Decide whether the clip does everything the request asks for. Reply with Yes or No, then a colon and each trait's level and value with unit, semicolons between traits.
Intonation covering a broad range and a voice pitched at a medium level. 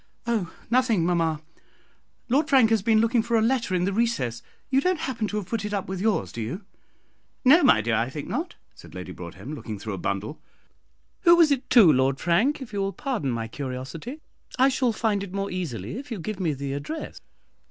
No: wide, 8.7 semitones; high, 200 Hz